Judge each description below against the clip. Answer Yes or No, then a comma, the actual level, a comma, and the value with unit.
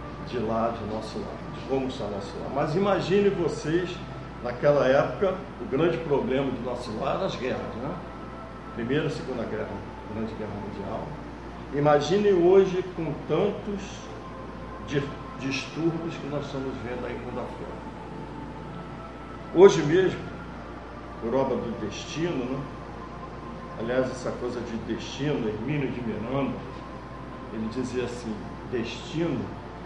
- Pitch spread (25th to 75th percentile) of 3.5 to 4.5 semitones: No, average, 5.2 semitones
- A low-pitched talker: Yes, low, 130 Hz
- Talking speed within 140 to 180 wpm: No, average, 130 wpm